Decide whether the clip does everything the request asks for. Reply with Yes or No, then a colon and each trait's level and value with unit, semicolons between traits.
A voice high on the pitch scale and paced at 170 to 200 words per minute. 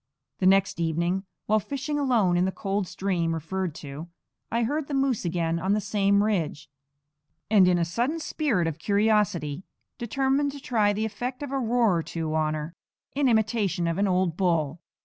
Yes: high, 195 Hz; average, 185 wpm